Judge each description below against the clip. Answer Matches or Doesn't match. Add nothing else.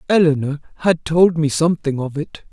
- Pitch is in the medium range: Matches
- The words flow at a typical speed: Matches